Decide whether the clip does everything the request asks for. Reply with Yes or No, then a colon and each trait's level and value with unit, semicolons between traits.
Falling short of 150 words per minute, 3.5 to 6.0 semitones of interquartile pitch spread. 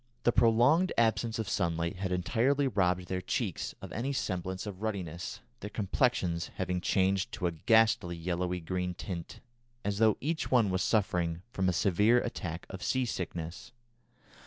No: average, 160 wpm; average, 4.1 semitones